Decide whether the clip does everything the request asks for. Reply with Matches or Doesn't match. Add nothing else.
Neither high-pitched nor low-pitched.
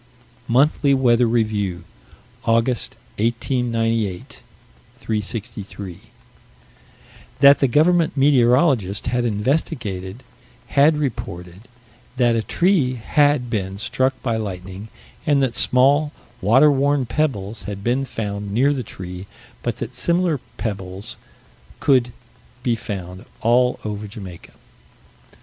Doesn't match